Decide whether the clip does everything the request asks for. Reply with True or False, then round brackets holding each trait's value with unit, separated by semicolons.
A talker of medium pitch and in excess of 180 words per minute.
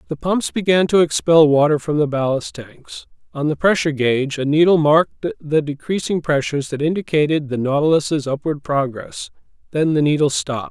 False (150 Hz; 170 wpm)